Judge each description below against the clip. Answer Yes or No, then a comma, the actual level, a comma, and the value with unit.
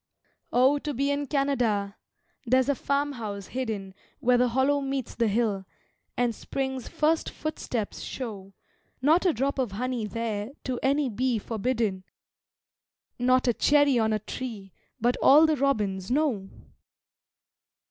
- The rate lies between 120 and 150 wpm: Yes, slow, 135 wpm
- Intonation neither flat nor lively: Yes, average, 4.3 semitones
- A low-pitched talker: No, very high, 250 Hz